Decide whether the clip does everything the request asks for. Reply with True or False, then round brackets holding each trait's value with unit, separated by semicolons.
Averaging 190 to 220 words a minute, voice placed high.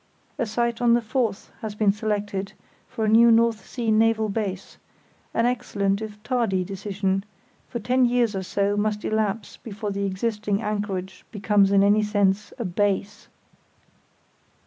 False (145 wpm; 210 Hz)